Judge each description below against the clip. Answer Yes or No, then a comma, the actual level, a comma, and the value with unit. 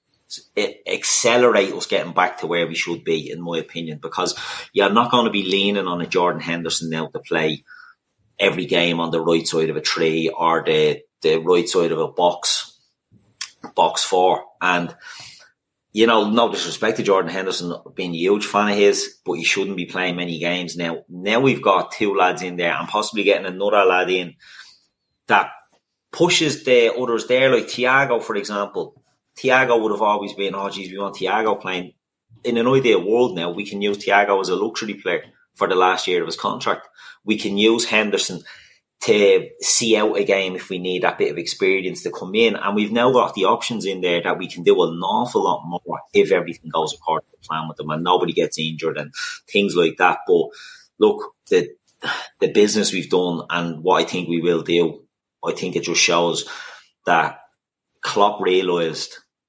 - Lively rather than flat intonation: Yes, wide, 6.6 semitones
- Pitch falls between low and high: No, low, 100 Hz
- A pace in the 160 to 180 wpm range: No, average, 195 wpm